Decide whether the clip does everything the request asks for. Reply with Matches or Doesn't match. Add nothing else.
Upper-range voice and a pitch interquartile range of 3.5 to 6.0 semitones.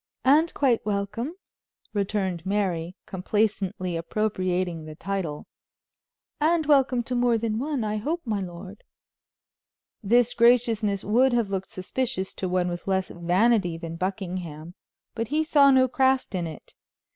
Matches